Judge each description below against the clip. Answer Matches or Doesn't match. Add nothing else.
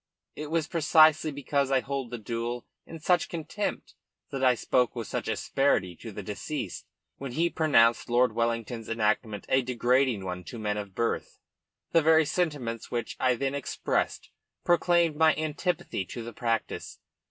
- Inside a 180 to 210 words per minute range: Doesn't match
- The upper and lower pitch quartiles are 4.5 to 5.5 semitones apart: Matches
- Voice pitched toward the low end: Matches